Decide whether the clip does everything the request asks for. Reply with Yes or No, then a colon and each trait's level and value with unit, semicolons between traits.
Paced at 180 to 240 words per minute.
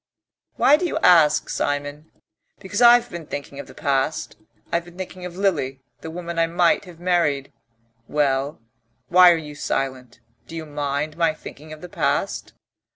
No: average, 165 wpm